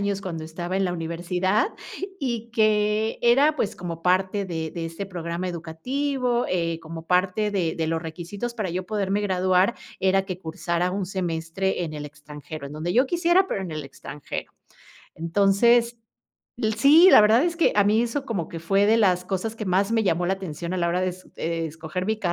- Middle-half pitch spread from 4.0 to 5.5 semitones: Yes, average, 4.3 semitones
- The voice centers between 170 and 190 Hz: Yes, medium, 185 Hz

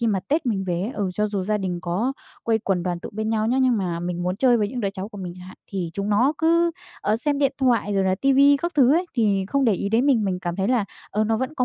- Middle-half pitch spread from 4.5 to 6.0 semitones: Yes, average, 5.1 semitones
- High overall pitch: Yes, high, 215 Hz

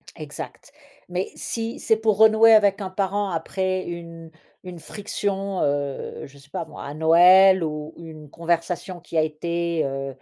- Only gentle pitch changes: No, average, 3.6 semitones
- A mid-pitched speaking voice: Yes, medium, 170 Hz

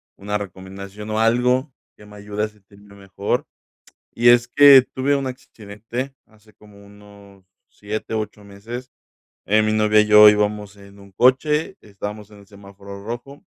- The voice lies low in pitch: Yes, low, 105 Hz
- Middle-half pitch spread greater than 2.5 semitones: Yes, average, 2.9 semitones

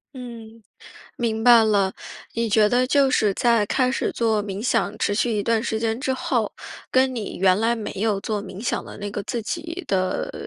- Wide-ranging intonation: No, average, 2.8 semitones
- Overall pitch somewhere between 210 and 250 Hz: Yes, high, 225 Hz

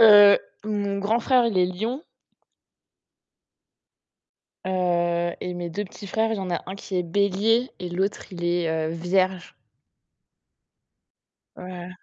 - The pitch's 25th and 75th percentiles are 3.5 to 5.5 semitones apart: No, average, 2.8 semitones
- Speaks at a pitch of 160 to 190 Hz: Yes, medium, 185 Hz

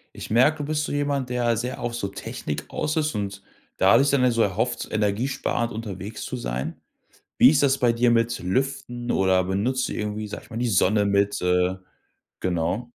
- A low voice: Yes, low, 115 Hz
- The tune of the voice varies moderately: Yes, average, 4.3 semitones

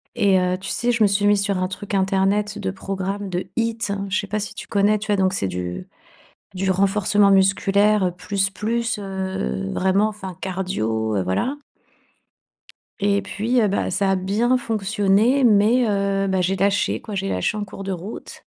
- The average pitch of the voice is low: No, high, 195 Hz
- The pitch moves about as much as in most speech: No, narrow, 1.7 semitones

